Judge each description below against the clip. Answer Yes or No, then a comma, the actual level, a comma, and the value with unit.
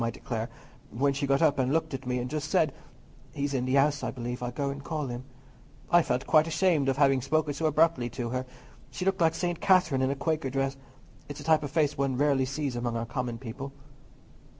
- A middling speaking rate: No, fast, 230 wpm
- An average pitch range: Yes, average, 3.3 semitones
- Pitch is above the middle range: No, medium, 140 Hz